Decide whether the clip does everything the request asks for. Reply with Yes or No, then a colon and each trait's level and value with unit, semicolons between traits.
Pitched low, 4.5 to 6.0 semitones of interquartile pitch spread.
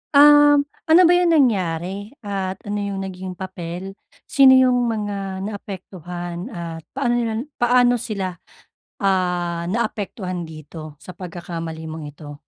No: high, 190 Hz; average, 5.2 semitones